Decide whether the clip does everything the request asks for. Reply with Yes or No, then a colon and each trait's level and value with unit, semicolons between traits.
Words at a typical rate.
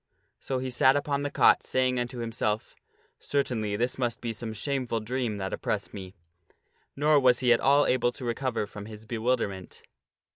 Yes: average, 180 wpm